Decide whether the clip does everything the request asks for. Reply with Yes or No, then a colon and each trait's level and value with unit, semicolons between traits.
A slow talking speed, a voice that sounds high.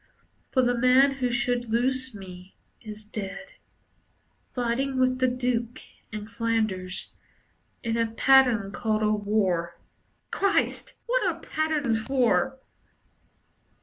Yes: slow, 115 wpm; high, 235 Hz